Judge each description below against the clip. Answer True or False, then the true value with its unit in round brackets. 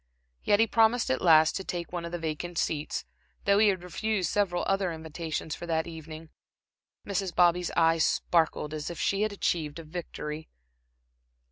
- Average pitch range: True (3.3 semitones)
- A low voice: False (170 Hz)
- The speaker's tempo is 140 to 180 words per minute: True (170 wpm)